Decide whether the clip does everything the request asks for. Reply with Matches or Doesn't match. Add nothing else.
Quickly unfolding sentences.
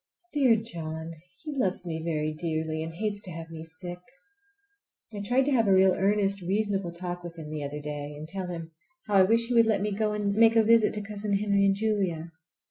Matches